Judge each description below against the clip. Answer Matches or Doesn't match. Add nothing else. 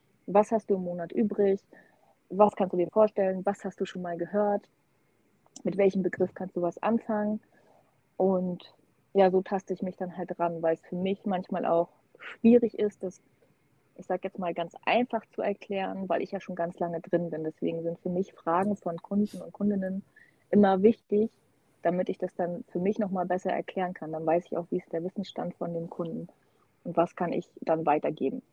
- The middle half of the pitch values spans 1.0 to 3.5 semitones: Matches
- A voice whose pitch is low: Doesn't match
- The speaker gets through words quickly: Matches